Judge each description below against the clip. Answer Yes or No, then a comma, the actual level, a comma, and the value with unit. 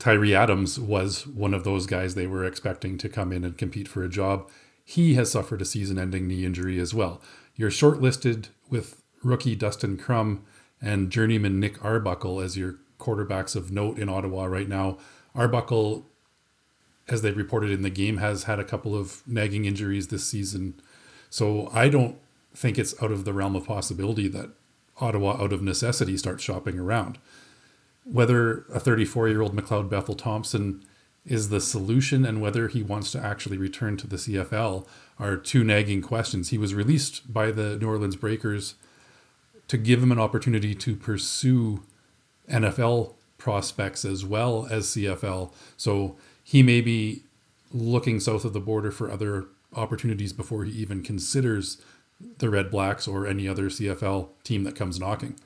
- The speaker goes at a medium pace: Yes, average, 170 wpm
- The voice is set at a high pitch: No, low, 105 Hz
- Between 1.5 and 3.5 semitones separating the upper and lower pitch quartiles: Yes, average, 3.0 semitones